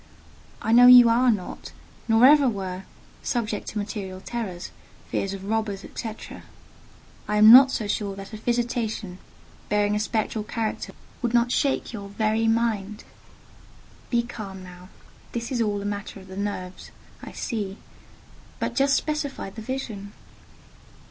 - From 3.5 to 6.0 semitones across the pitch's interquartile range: No, average, 3.0 semitones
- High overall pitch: Yes, high, 215 Hz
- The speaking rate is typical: Yes, average, 150 wpm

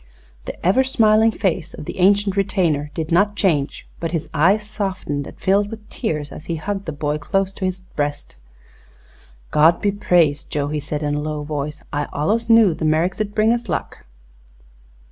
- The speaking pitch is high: No, medium, 175 Hz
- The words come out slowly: No, average, 185 wpm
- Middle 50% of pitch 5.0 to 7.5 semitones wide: Yes, average, 5.3 semitones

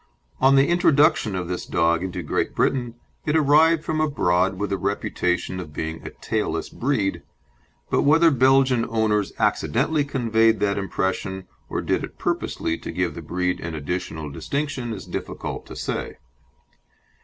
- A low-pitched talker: Yes, low, 110 Hz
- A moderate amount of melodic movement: No, wide, 7.5 semitones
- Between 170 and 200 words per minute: No, average, 155 wpm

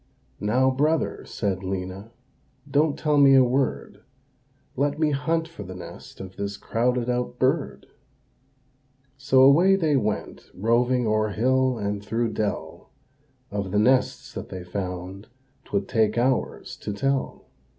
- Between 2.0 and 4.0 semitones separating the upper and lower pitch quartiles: No, average, 5.1 semitones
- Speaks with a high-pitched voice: No, low, 120 Hz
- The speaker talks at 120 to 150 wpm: Yes, average, 140 wpm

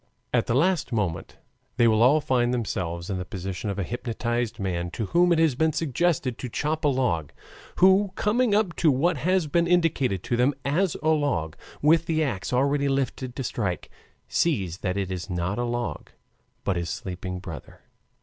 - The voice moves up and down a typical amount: No, wide, 8.6 semitones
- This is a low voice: Yes, low, 125 Hz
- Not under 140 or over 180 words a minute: No, average, 190 wpm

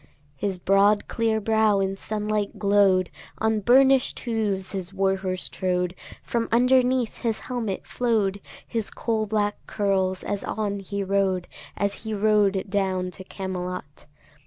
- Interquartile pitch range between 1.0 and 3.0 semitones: Yes, narrow, 2.4 semitones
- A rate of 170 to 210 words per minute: No, slow, 135 wpm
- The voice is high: Yes, high, 200 Hz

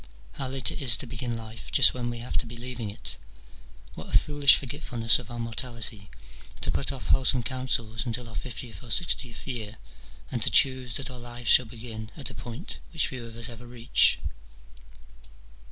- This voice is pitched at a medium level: No, low, 120 Hz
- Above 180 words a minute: Yes, average, 200 wpm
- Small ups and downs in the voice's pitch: Yes, narrow, 2.1 semitones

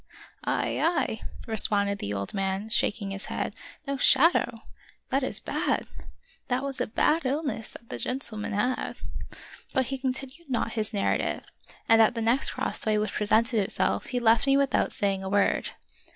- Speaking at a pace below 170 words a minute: No, average, 180 wpm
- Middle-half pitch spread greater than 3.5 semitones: Yes, average, 4.3 semitones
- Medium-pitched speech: No, high, 230 Hz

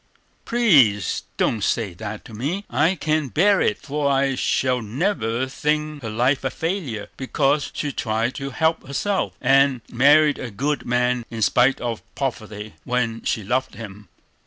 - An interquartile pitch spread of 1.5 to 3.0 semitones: No, average, 4.7 semitones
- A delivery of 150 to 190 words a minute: Yes, average, 160 wpm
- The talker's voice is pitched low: Yes, low, 130 Hz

